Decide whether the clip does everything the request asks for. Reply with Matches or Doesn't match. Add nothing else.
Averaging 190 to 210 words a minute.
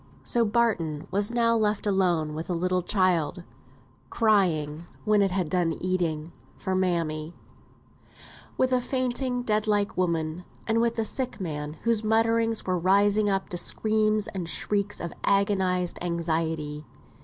Doesn't match